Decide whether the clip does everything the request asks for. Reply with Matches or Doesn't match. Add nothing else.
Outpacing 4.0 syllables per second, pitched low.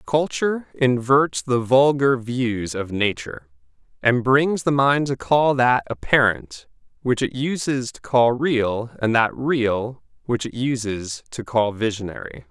Doesn't match